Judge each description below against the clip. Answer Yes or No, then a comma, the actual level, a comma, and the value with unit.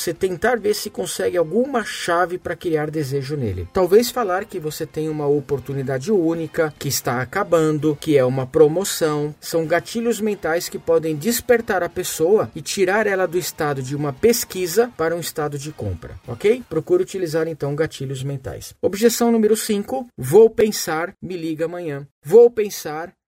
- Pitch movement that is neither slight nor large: No, wide, 5.9 semitones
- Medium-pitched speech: Yes, medium, 170 Hz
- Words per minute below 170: Yes, average, 160 wpm